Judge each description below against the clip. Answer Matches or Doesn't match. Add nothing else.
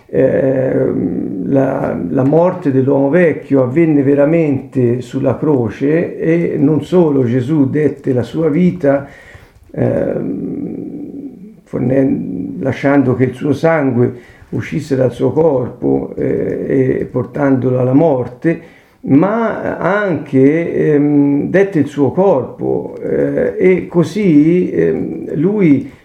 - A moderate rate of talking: Doesn't match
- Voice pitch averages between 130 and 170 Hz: Matches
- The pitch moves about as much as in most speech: Matches